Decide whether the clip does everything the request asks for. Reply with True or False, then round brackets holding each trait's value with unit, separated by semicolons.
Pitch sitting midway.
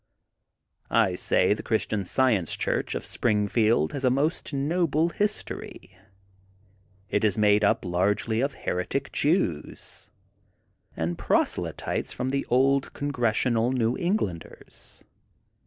False (120 Hz)